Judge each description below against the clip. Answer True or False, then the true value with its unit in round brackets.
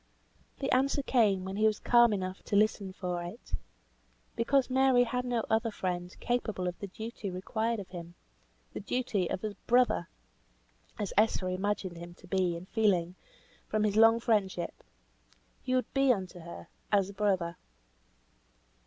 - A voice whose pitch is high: True (205 Hz)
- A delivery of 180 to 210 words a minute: False (160 wpm)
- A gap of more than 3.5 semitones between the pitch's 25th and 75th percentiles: True (4.1 semitones)